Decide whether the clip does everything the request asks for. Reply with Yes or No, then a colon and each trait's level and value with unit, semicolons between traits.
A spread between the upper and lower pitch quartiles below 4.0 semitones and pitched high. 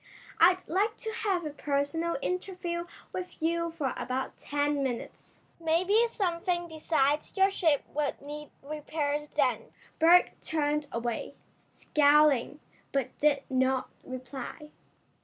Yes: average, 3.4 semitones; very high, 300 Hz